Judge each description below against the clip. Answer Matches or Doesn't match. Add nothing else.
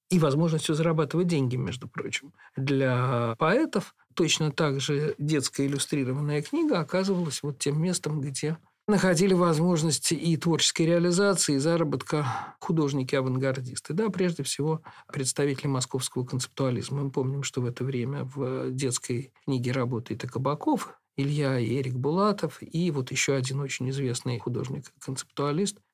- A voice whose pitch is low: Doesn't match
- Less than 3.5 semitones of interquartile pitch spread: Doesn't match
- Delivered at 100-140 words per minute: Matches